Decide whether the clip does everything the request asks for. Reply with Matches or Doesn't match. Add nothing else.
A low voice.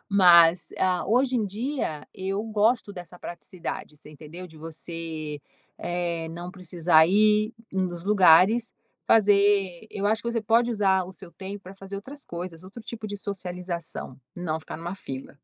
Doesn't match